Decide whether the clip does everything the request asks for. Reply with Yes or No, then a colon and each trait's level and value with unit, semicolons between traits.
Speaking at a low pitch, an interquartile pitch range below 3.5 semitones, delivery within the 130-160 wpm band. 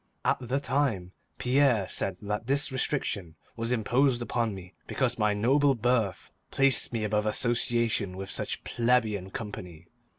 No: low, 115 Hz; average, 3.8 semitones; average, 140 wpm